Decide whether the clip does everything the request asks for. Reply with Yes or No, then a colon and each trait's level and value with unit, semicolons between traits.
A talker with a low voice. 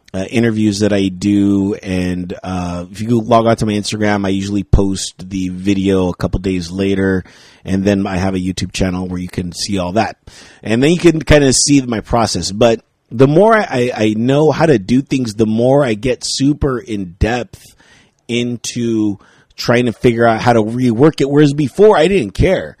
Yes: low, 110 Hz